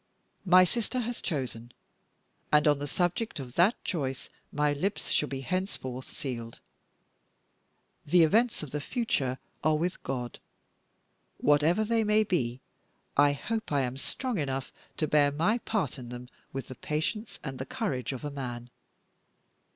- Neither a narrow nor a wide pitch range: No, wide, 6.6 semitones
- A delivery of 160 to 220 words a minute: No, average, 150 wpm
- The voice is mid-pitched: Yes, medium, 150 Hz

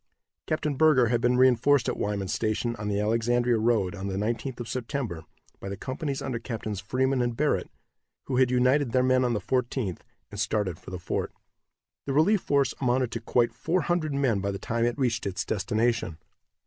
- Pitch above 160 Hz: No, low, 120 Hz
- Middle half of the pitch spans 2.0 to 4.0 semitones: Yes, average, 3.6 semitones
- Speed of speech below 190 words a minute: No, average, 195 wpm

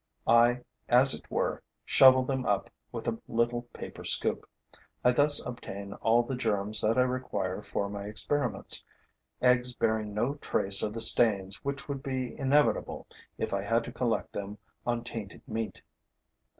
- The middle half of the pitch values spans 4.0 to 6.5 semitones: No, average, 3.4 semitones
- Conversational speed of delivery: Yes, average, 160 wpm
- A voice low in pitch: Yes, low, 115 Hz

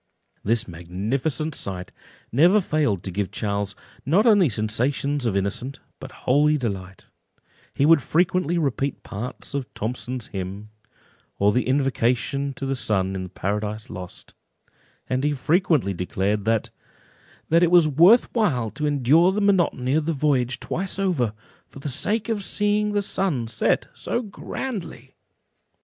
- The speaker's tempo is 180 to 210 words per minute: No, average, 145 wpm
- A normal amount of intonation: No, wide, 7.6 semitones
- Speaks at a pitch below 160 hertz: Yes, low, 135 Hz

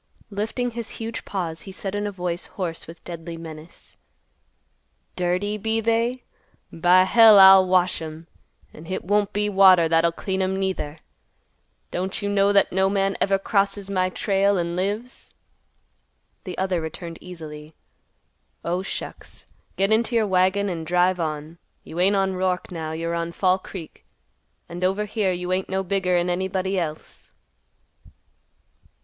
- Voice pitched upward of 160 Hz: Yes, medium, 185 Hz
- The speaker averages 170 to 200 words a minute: No, average, 150 wpm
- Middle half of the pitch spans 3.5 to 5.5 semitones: No, narrow, 2.6 semitones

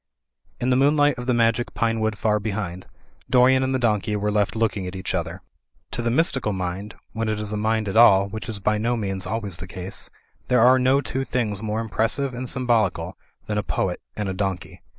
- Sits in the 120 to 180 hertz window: No, low, 110 Hz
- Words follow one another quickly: Yes, fast, 215 wpm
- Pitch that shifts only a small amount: No, average, 3.6 semitones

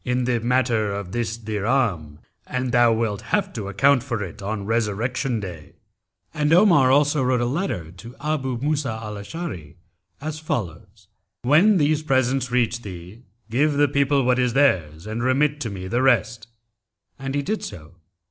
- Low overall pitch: Yes, low, 120 Hz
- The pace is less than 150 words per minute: No, average, 165 wpm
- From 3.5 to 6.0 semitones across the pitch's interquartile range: Yes, average, 5.0 semitones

